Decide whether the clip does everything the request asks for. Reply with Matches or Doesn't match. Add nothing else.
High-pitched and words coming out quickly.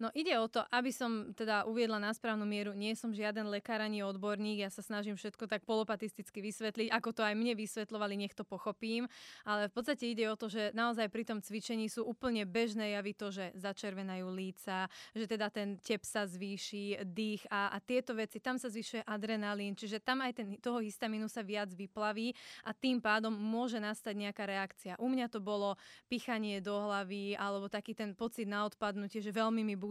Matches